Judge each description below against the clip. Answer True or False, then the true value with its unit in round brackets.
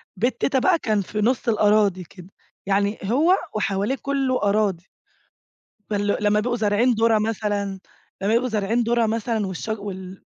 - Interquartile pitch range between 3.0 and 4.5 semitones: False (2.6 semitones)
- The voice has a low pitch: False (215 Hz)